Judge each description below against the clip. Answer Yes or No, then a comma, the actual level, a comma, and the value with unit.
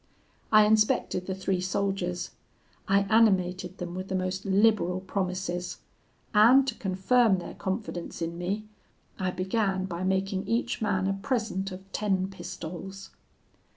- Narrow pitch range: Yes, narrow, 2.1 semitones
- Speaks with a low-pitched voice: No, high, 190 Hz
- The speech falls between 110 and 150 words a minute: Yes, slow, 135 wpm